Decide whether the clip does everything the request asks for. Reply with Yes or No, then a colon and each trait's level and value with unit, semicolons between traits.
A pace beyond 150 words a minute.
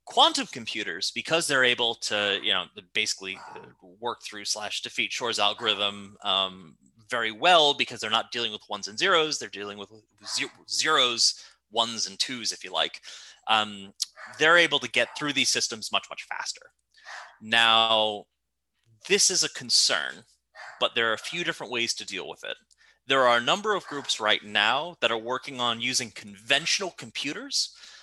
Yes: average, 165 wpm